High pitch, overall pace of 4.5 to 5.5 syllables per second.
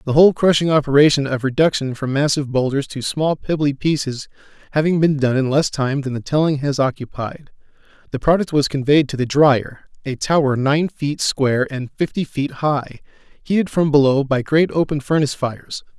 No: medium, 140 Hz; 5.4 syllables/s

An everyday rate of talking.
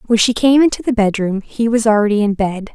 No: fast, 240 wpm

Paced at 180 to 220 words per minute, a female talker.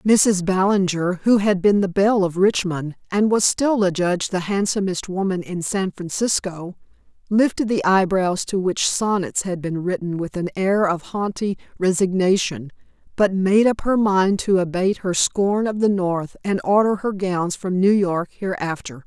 No: average, 170 wpm; female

